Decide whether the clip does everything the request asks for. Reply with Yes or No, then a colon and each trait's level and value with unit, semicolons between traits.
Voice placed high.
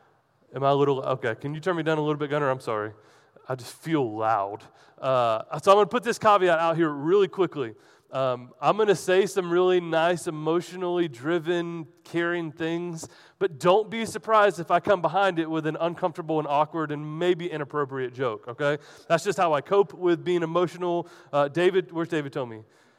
No: medium, 165 Hz